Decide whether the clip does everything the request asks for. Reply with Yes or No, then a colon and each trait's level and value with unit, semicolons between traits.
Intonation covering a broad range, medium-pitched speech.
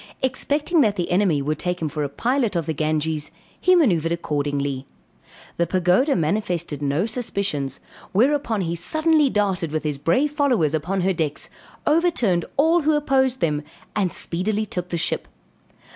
Yes: wide, 8.6 semitones; medium, 180 Hz